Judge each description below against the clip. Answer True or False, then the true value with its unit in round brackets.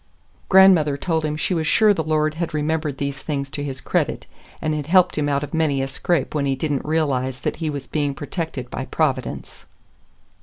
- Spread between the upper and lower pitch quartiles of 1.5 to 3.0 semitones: True (2.4 semitones)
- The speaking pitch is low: False (150 Hz)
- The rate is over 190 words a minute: True (205 wpm)